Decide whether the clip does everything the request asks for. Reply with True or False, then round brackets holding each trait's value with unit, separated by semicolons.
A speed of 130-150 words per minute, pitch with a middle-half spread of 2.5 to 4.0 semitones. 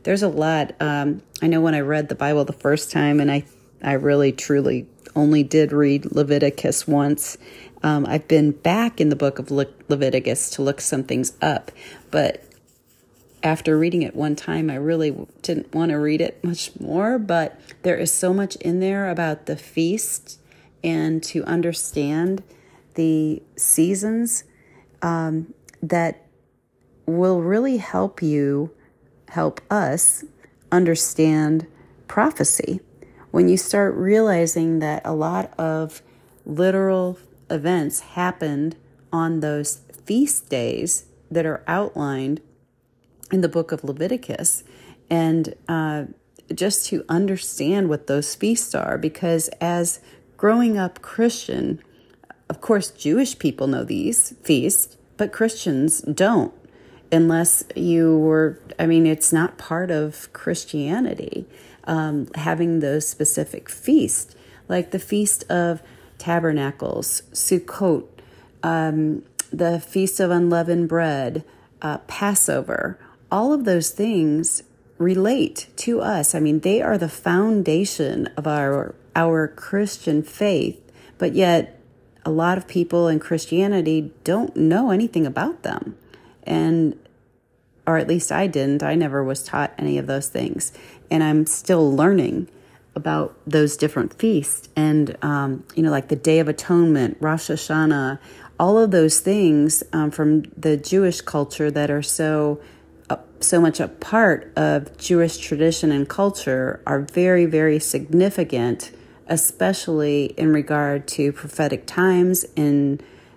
True (135 wpm; 3.2 semitones)